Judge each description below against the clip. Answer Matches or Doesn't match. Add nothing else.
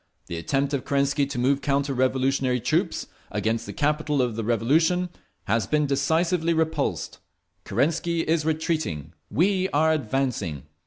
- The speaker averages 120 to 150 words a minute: Matches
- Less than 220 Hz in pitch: Matches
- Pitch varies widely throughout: Doesn't match